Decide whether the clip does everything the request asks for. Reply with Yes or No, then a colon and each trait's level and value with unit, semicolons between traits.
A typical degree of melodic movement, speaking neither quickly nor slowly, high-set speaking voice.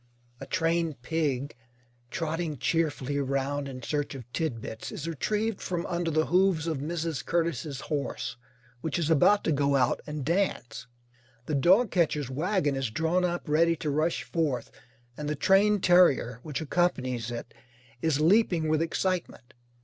No: average, 3.7 semitones; average, 150 wpm; medium, 155 Hz